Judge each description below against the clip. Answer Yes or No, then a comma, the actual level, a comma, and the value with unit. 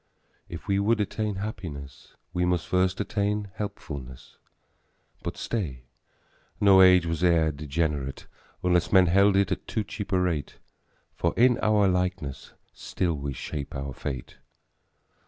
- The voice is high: No, very low, 90 Hz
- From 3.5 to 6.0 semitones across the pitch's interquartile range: Yes, average, 4.9 semitones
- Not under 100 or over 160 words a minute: Yes, slow, 135 wpm